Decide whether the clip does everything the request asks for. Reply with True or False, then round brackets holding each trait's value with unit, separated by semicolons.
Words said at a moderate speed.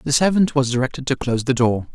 False (245 wpm)